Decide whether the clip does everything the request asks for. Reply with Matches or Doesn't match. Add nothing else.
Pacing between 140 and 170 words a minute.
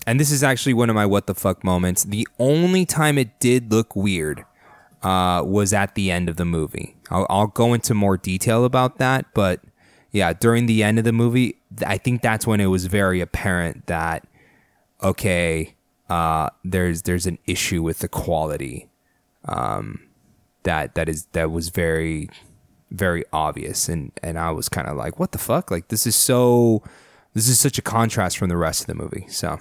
Doesn't match